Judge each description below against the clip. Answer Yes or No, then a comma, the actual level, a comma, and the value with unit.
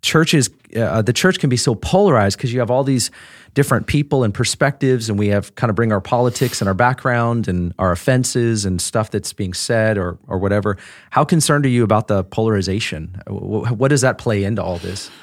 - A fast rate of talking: Yes, fast, 210 wpm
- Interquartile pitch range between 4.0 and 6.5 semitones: Yes, average, 4.4 semitones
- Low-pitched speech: Yes, low, 115 Hz